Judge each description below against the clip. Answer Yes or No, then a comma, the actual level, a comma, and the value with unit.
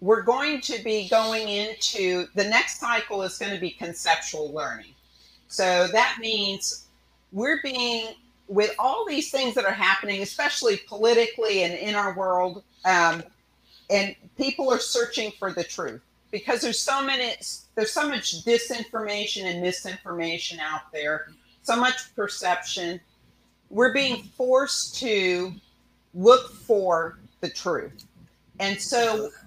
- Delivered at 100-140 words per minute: Yes, slow, 135 wpm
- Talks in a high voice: Yes, high, 205 Hz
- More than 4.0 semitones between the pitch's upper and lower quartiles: Yes, average, 4.9 semitones